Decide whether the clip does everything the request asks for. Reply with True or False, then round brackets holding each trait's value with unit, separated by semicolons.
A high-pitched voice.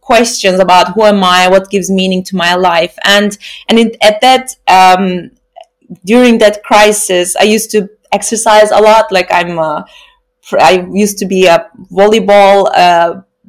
True (205 Hz)